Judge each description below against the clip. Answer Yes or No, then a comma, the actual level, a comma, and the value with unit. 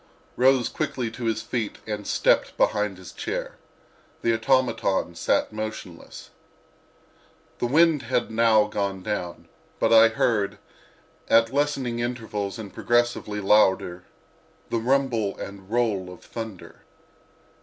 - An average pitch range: Yes, average, 3.0 semitones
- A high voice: No, low, 110 Hz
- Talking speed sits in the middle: No, slow, 120 wpm